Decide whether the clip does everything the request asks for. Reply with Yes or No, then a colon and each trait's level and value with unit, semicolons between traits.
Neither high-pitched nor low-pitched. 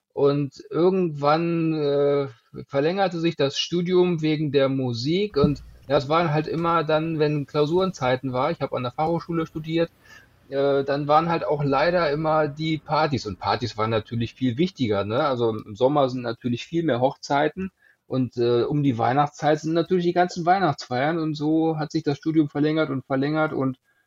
Yes: medium, 150 Hz